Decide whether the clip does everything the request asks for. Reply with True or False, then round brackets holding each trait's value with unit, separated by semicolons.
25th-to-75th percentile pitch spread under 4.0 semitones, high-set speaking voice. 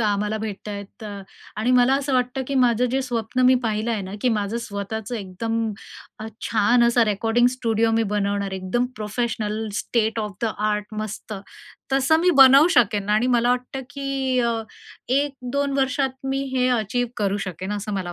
True (3.3 semitones; 230 Hz)